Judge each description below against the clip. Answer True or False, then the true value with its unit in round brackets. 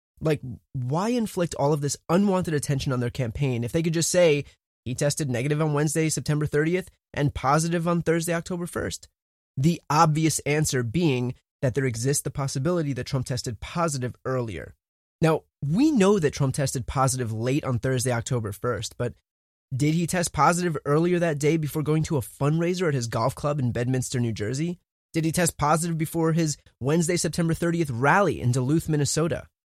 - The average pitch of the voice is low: False (145 Hz)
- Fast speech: False (180 wpm)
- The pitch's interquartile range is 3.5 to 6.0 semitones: True (4.2 semitones)